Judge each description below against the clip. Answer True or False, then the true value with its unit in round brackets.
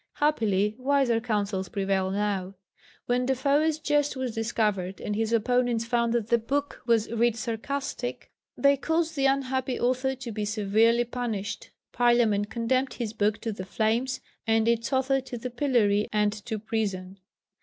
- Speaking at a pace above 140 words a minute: True (155 wpm)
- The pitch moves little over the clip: False (3.7 semitones)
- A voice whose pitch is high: True (235 Hz)